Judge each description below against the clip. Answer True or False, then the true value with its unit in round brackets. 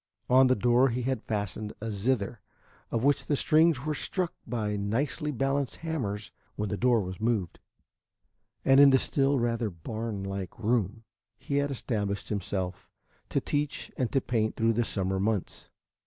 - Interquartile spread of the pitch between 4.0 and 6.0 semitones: True (4.6 semitones)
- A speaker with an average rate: True (165 wpm)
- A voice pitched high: False (115 Hz)